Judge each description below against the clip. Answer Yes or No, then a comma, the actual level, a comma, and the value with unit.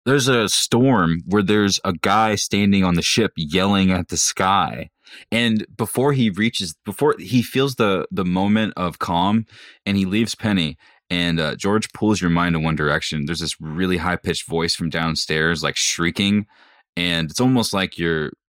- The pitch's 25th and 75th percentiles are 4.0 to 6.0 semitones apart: Yes, average, 4.7 semitones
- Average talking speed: Yes, average, 180 wpm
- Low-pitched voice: Yes, very low, 95 Hz